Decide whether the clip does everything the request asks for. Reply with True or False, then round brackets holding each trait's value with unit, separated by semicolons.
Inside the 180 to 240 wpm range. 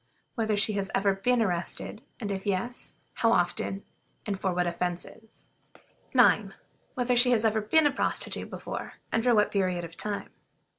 False (165 wpm)